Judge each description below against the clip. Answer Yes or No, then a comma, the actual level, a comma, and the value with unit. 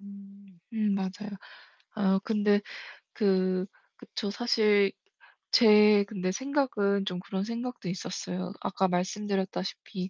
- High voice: Yes, high, 200 Hz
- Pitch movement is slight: Yes, narrow, 1.9 semitones